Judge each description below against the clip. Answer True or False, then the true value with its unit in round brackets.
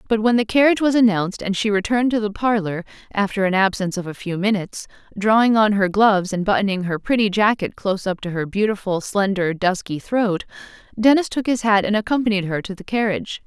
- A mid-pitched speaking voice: False (205 Hz)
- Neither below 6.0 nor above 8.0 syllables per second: True (6.2 syllables/s)